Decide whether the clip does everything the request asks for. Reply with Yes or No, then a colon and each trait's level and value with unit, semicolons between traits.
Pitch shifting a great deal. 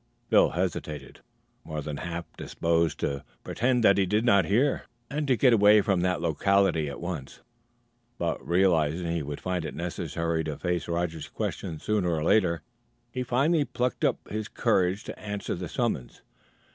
No: average, 4.4 semitones